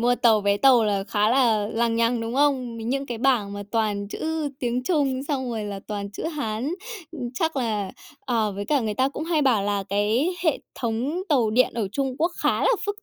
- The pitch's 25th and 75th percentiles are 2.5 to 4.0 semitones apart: No, average, 4.4 semitones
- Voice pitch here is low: No, high, 235 Hz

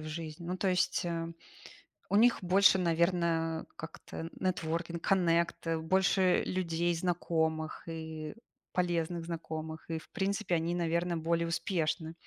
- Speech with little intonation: Yes, narrow, 1.8 semitones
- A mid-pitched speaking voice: Yes, medium, 170 Hz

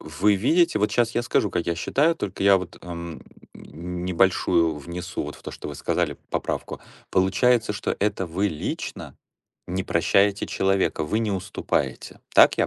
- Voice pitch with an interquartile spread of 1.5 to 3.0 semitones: No, average, 3.4 semitones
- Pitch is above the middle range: No, very low, 95 Hz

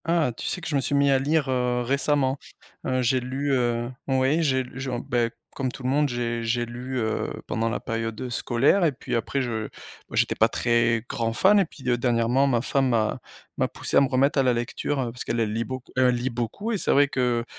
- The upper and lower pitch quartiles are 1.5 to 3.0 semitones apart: Yes, average, 2.7 semitones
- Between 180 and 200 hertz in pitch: No, low, 125 Hz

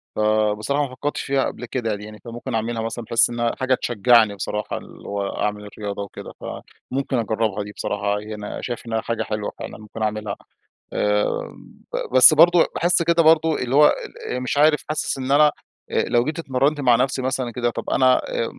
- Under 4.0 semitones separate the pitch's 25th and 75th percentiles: No, average, 4.4 semitones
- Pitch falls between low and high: No, low, 120 Hz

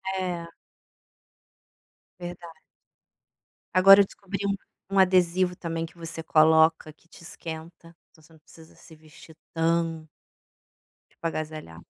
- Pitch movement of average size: No, narrow, 2.0 semitones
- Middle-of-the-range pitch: Yes, medium, 165 Hz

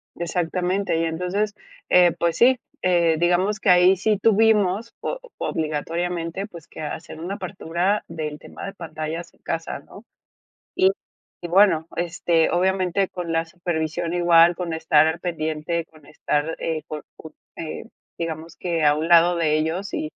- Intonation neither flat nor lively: No, narrow, 2.3 semitones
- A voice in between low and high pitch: Yes, medium, 170 Hz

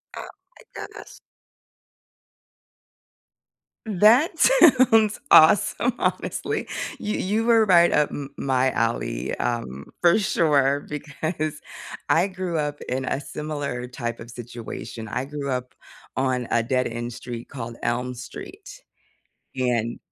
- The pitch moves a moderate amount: No, wide, 6.1 semitones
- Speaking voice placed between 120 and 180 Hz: Yes, medium, 140 Hz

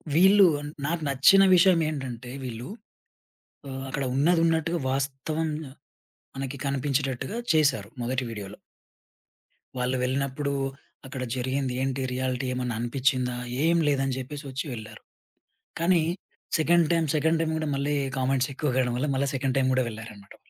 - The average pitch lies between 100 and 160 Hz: Yes, low, 135 Hz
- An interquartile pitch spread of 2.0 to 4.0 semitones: Yes, average, 3.4 semitones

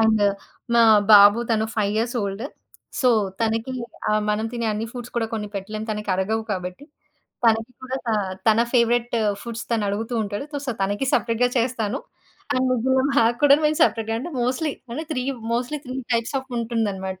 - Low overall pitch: No, high, 230 Hz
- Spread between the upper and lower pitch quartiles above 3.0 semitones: No, average, 2.7 semitones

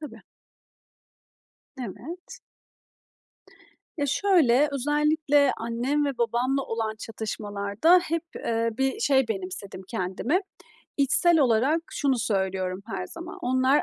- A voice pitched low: No, very high, 260 Hz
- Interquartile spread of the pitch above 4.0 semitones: Yes, average, 5.0 semitones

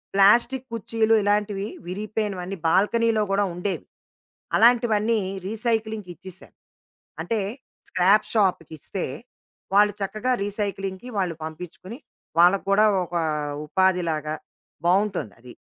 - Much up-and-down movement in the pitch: No, average, 3.1 semitones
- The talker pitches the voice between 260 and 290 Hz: No, high, 200 Hz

